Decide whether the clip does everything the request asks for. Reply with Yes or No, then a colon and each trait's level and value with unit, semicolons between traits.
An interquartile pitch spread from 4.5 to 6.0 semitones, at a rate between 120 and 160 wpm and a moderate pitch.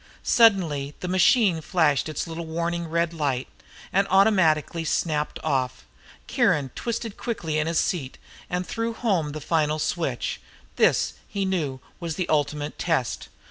No: average, 3.7 semitones; average, 140 wpm; medium, 165 Hz